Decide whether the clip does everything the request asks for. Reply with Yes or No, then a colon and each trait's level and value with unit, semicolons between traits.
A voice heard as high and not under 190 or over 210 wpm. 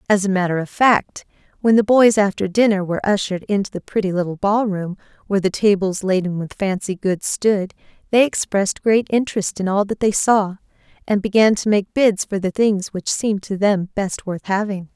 Yes: high, 200 Hz; average, 195 wpm